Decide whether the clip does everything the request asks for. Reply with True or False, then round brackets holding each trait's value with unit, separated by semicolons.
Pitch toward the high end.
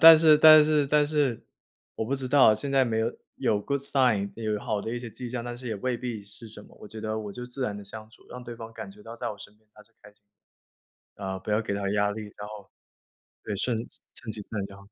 False (115 Hz)